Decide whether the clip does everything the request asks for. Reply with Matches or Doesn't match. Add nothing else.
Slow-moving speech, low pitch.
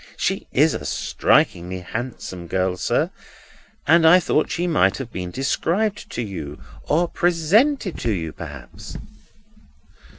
Matches